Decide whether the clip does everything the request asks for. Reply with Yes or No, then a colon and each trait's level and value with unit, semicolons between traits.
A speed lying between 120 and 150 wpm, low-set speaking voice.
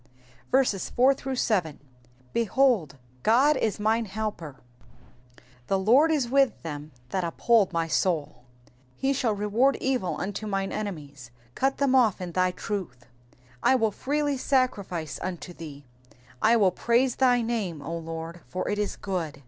No: average, 145 wpm; high, 205 Hz